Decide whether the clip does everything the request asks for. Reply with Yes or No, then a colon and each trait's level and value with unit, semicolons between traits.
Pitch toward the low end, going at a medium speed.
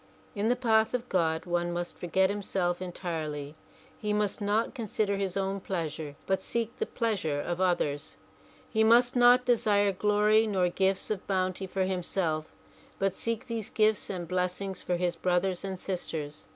No: high, 190 Hz; average, 165 wpm